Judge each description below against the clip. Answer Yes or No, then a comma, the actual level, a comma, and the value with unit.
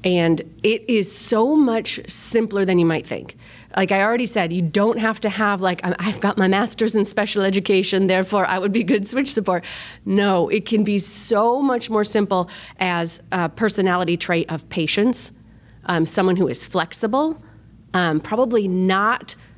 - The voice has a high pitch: Yes, high, 195 Hz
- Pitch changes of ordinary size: Yes, average, 3.4 semitones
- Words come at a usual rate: Yes, average, 170 wpm